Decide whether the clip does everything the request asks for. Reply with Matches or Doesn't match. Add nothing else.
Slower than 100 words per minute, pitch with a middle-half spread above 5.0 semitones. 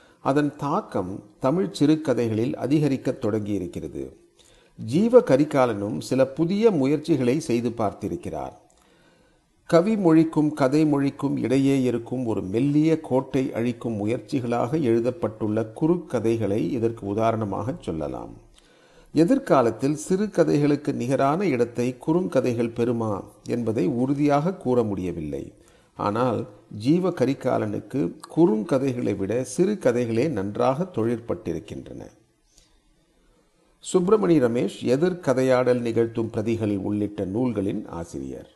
Matches